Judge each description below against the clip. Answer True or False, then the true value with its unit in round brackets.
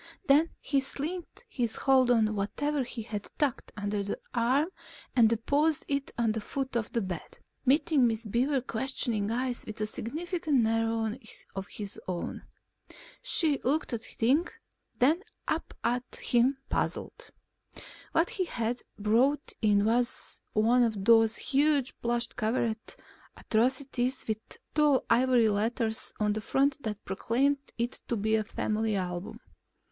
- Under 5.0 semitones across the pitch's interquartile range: True (4.1 semitones)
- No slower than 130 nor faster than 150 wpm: True (145 wpm)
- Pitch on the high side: True (235 Hz)